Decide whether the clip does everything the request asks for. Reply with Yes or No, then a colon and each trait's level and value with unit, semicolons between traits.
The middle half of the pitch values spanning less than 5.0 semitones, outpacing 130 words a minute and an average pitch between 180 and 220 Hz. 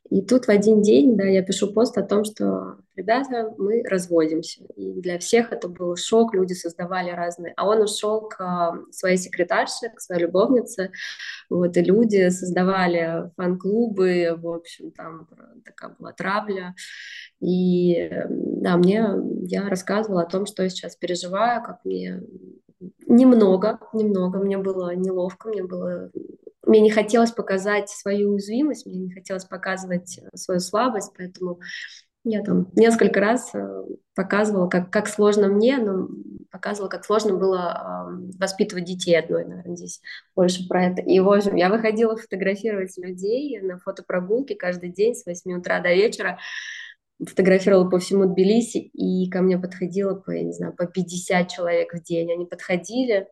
Yes: average, 2.9 semitones; average, 150 wpm; high, 190 Hz